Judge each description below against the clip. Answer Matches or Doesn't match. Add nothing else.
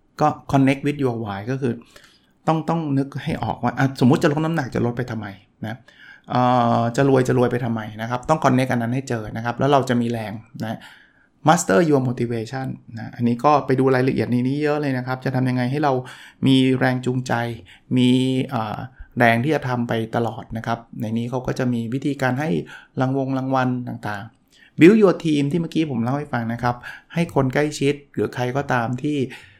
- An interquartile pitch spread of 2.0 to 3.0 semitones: Matches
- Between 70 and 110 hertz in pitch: Doesn't match